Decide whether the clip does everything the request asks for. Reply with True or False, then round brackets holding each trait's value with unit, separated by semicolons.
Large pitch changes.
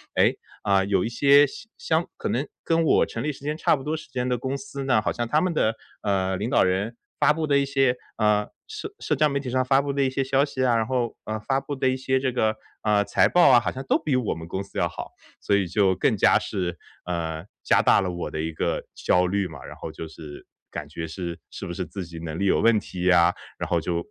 True (6.7 semitones)